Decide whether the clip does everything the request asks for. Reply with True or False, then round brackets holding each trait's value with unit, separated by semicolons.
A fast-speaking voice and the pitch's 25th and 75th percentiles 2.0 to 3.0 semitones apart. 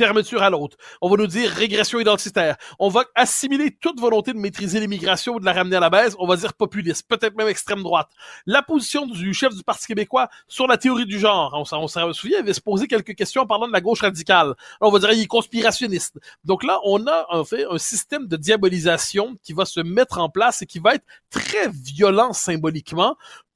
False (225 wpm; 4.3 semitones)